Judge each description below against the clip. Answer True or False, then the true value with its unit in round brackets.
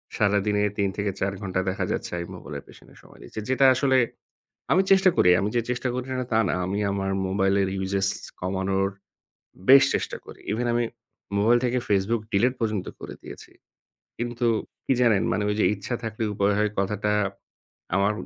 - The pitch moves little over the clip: False (3.5 semitones)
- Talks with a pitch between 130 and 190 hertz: False (105 Hz)